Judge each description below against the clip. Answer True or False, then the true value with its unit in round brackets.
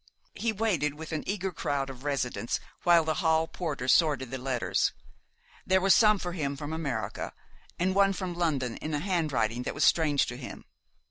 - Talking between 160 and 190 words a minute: True (185 wpm)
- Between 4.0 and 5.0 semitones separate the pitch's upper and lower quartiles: True (4.7 semitones)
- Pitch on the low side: False (155 Hz)